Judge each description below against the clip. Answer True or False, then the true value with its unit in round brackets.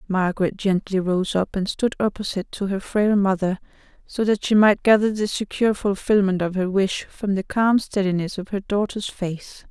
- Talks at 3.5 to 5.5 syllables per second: True (5.0 syllables/s)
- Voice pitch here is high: True (195 Hz)